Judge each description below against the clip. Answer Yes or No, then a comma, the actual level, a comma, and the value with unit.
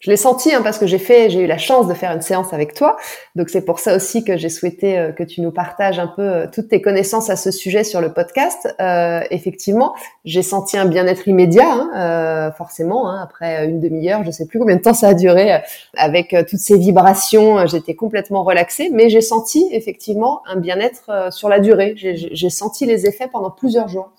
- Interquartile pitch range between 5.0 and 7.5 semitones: No, average, 3.6 semitones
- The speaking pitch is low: No, high, 190 Hz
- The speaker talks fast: Yes, fast, 230 wpm